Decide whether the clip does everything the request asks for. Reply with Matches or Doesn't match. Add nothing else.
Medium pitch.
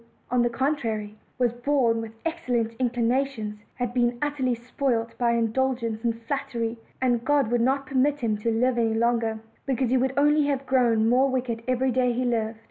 Doesn't match